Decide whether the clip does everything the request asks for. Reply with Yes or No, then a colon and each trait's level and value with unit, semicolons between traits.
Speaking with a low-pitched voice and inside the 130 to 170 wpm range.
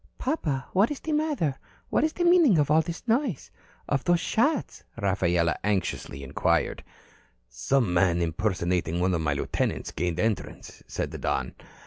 Yes: low, 120 Hz; average, 155 wpm